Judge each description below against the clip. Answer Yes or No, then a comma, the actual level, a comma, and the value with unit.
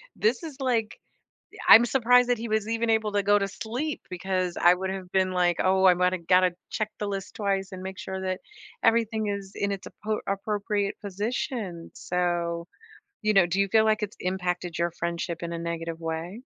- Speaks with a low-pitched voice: No, high, 195 Hz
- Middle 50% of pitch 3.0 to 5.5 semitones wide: Yes, average, 3.3 semitones